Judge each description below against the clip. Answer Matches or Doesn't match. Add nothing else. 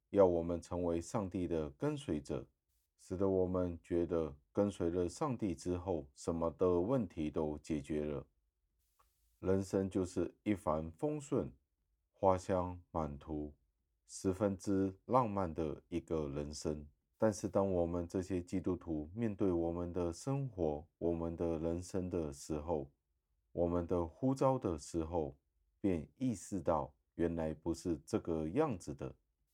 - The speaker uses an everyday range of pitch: Matches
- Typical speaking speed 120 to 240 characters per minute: Matches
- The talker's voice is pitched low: Matches